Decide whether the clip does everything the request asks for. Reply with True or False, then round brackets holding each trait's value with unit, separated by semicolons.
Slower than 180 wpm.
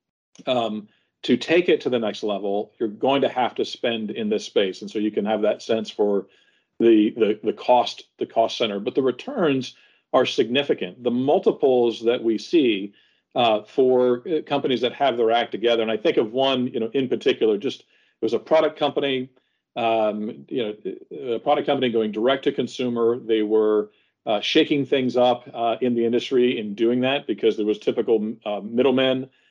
False (190 wpm)